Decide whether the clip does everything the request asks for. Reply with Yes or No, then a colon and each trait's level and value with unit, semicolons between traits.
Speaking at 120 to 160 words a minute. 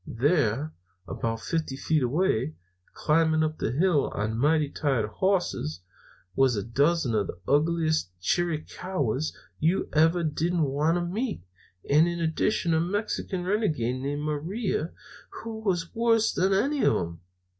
Yes: average, 140 wpm